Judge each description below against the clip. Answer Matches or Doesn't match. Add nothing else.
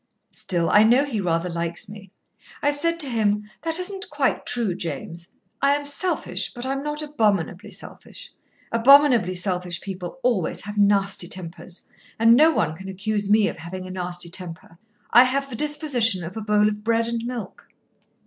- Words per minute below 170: Doesn't match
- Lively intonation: Matches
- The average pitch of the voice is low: Doesn't match